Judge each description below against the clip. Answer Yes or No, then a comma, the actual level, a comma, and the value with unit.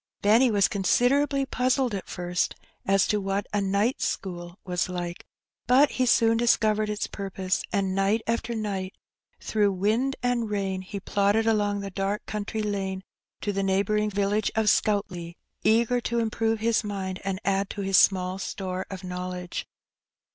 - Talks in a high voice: Yes, high, 205 Hz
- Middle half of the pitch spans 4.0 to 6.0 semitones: No, average, 2.7 semitones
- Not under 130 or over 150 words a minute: No, average, 165 wpm